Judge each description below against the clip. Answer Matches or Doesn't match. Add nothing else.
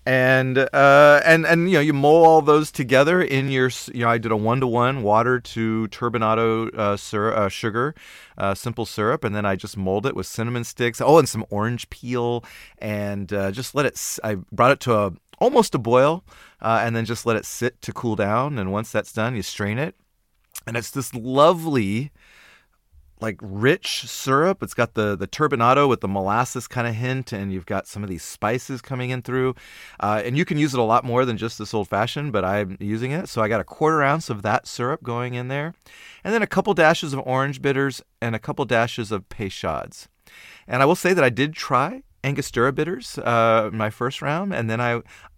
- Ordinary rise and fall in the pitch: Matches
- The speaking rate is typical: Doesn't match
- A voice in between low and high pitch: Doesn't match